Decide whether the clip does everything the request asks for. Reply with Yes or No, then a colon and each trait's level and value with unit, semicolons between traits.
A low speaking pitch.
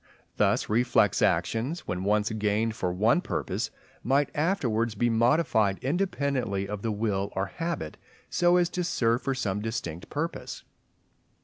Yes: low, 115 Hz